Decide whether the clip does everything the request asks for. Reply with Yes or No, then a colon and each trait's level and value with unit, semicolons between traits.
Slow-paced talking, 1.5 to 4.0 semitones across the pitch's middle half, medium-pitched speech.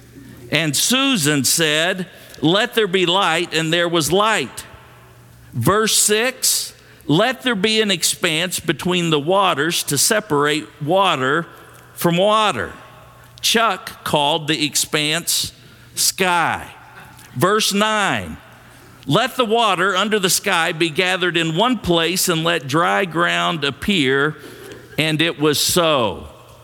No: slow, 120 wpm; average, 5.2 semitones; medium, 170 Hz